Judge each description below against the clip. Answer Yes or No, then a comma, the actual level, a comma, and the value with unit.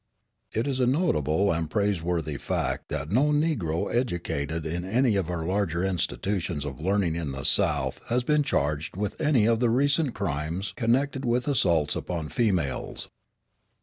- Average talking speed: Yes, average, 155 wpm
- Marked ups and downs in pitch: Yes, wide, 7.2 semitones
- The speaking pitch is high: No, very low, 95 Hz